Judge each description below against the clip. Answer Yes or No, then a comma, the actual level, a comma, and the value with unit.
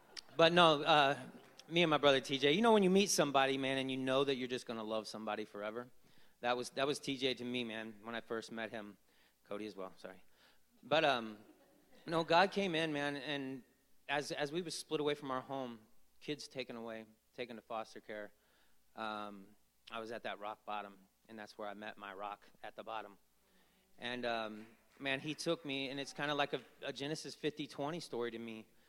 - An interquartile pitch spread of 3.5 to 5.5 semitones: Yes, average, 4.7 semitones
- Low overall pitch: Yes, low, 125 Hz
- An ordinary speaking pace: No, fast, 215 wpm